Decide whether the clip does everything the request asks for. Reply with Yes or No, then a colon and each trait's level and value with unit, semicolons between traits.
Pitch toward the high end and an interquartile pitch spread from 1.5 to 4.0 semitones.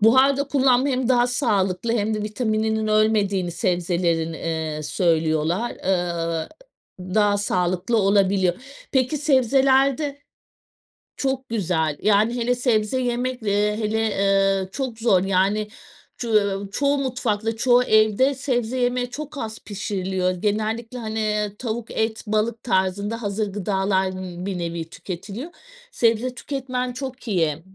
No: high, 215 Hz; average, 4.6 semitones